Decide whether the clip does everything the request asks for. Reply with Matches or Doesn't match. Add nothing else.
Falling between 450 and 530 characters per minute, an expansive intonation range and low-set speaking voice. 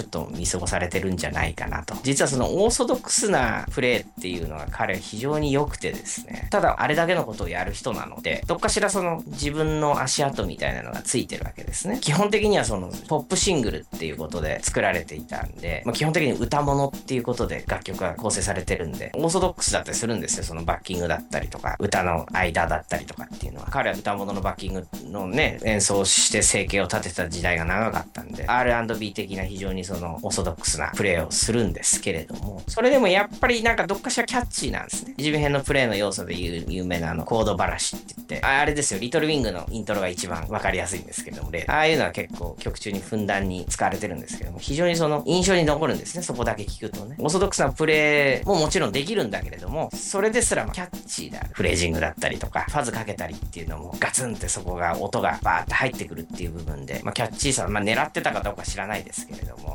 Matches